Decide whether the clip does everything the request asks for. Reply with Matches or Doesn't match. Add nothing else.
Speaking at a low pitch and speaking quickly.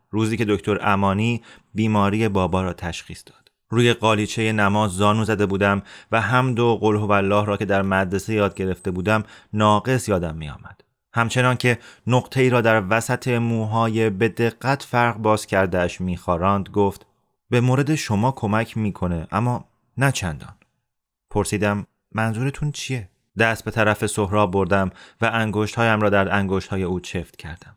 Matches